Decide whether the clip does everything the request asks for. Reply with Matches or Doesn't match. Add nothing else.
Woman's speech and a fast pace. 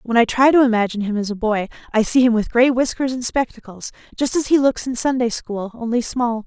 Matches